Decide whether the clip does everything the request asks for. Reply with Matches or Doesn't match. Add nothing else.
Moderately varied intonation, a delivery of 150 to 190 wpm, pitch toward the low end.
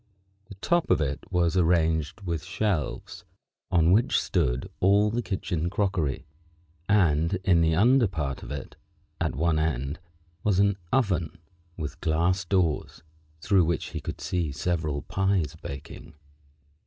Doesn't match